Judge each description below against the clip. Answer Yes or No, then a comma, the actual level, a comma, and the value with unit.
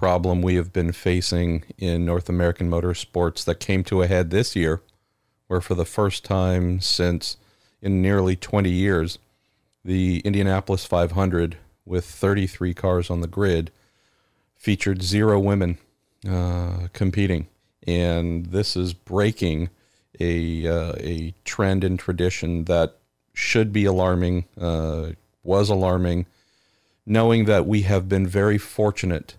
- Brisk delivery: No, slow, 135 wpm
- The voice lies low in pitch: Yes, very low, 90 Hz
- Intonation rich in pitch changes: No, narrow, 2.4 semitones